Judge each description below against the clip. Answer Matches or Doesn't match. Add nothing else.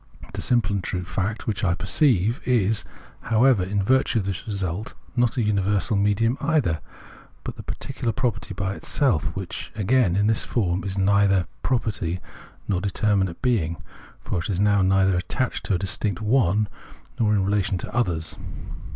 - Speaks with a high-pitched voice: Doesn't match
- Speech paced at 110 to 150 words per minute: Doesn't match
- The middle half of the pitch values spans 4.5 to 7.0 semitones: Doesn't match